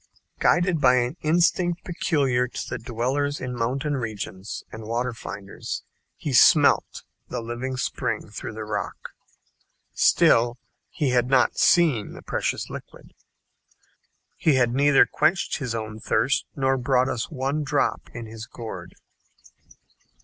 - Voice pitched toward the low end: Yes, low, 125 Hz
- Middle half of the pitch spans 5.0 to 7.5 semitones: No, average, 3.7 semitones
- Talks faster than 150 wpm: No, slow, 135 wpm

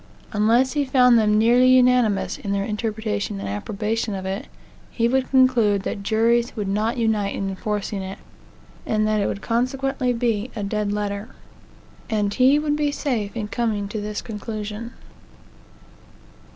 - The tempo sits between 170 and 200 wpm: No, average, 155 wpm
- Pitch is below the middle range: No, high, 220 Hz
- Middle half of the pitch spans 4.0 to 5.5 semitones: No, average, 2.9 semitones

